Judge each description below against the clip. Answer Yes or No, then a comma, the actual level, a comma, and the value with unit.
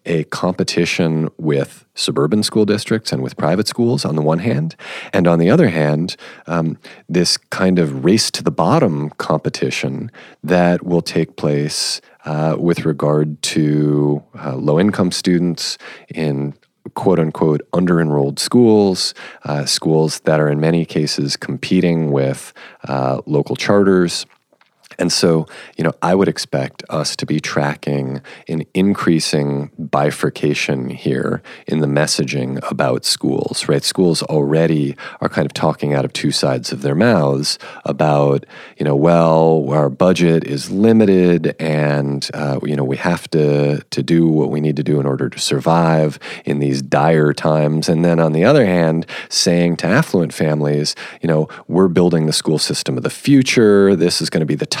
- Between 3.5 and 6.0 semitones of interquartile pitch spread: No, average, 2.9 semitones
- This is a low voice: Yes, very low, 80 Hz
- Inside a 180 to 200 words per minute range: No, average, 160 wpm